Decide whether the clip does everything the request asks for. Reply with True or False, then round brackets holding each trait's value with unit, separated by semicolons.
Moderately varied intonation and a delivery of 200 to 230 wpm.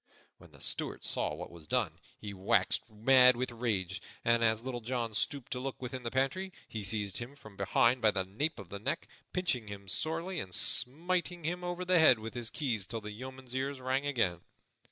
True (4.5 semitones; 205 wpm)